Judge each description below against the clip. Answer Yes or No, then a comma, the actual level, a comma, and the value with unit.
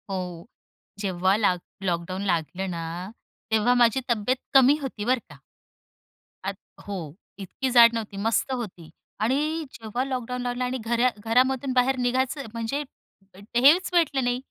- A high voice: Yes, high, 240 Hz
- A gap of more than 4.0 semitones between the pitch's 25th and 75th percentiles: Yes, average, 4.4 semitones